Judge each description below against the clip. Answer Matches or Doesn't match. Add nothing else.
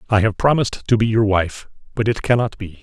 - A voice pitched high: Doesn't match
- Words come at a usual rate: Doesn't match